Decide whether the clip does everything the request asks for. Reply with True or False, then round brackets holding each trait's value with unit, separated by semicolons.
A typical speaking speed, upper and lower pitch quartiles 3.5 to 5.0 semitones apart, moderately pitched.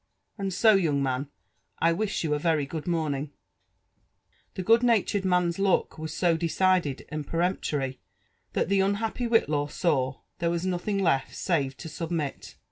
True (155 wpm; 4.5 semitones; 170 Hz)